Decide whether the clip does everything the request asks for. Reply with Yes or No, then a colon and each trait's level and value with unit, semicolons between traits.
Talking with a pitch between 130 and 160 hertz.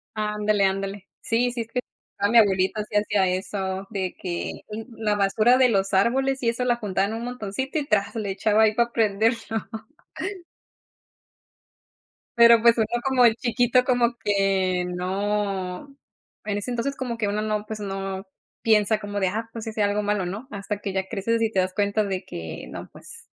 No: high, 210 Hz